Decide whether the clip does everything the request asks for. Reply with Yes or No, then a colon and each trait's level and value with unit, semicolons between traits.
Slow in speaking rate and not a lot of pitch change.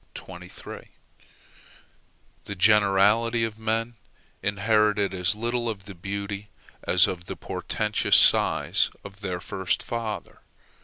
Yes: slow, 105 wpm; narrow, 2.3 semitones